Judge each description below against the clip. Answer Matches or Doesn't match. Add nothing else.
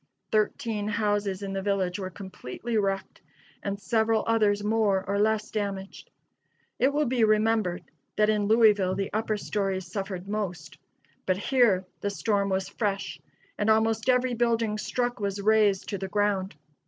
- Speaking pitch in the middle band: Doesn't match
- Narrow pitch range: Matches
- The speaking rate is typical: Matches